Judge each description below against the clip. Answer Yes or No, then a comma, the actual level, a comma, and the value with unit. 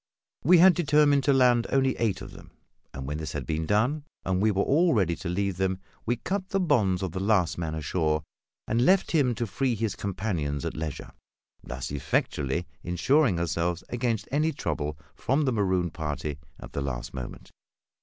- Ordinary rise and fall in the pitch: No, wide, 8.7 semitones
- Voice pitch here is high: No, very low, 95 Hz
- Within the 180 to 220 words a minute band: Yes, average, 185 wpm